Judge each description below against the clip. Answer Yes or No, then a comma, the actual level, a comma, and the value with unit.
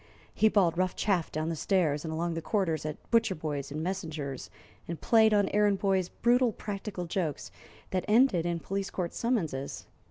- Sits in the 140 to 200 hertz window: Yes, medium, 185 Hz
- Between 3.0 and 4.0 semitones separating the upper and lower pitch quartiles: No, average, 4.4 semitones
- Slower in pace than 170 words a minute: No, average, 180 wpm